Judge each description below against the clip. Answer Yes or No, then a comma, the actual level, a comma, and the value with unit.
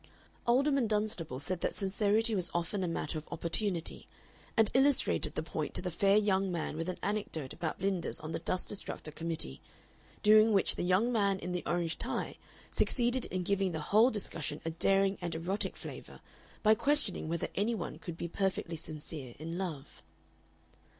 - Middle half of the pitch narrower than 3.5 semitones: No, average, 4.1 semitones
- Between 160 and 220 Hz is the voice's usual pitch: Yes, medium, 185 Hz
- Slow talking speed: No, average, 175 wpm